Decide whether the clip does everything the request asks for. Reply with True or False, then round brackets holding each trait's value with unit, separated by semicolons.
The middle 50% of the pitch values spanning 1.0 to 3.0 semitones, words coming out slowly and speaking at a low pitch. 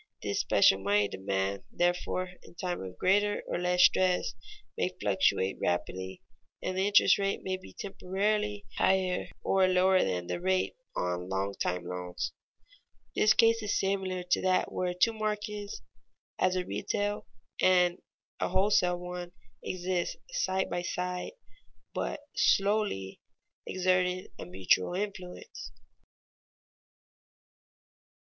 False (2.6 semitones; 120 wpm; 185 Hz)